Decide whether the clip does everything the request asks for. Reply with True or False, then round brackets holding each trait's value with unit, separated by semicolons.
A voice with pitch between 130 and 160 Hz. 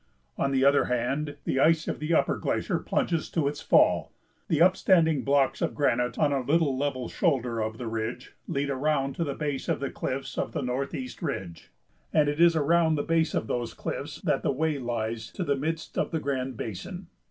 True (140 Hz)